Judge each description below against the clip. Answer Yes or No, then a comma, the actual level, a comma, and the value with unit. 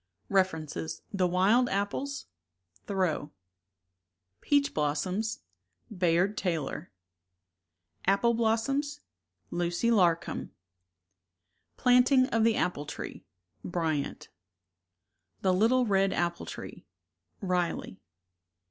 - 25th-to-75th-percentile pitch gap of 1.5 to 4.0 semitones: No, average, 5.0 semitones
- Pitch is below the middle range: No, high, 190 Hz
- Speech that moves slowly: Yes, slow, 85 wpm